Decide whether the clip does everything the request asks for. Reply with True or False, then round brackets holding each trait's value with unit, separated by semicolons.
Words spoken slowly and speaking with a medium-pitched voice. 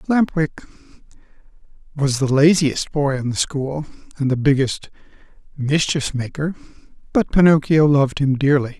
True (130 wpm; 145 Hz)